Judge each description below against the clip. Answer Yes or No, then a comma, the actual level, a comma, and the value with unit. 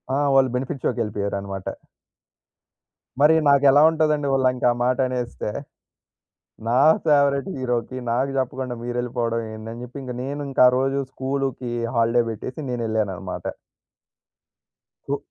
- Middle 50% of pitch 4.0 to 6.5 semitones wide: No, average, 2.7 semitones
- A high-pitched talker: No, low, 125 Hz